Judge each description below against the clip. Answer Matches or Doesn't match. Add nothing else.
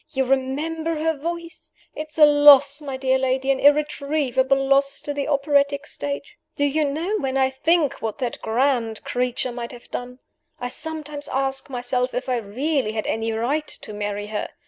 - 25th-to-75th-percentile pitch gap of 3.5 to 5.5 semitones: Doesn't match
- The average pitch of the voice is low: Doesn't match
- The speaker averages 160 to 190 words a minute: Matches